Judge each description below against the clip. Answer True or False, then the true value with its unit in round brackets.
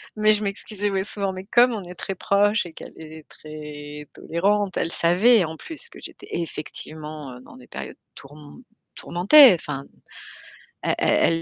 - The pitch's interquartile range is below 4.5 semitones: False (5.2 semitones)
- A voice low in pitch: False (180 Hz)